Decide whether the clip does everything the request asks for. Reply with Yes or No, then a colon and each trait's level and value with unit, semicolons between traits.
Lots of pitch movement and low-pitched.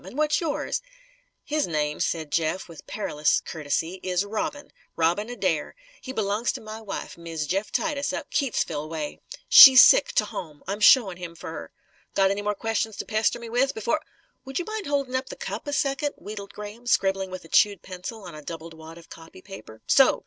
No: wide, 6.8 semitones; high, 200 Hz